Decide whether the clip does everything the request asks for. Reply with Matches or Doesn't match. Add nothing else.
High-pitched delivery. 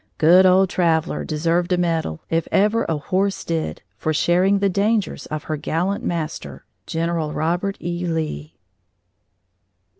Doesn't match